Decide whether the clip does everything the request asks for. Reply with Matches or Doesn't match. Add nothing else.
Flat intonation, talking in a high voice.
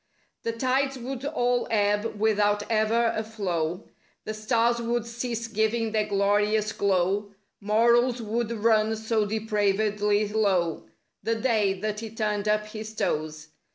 Matches